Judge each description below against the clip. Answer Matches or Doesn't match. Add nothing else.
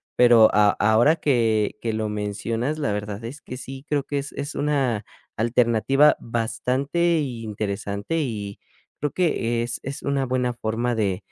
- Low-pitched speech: Matches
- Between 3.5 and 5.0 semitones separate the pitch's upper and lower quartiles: Matches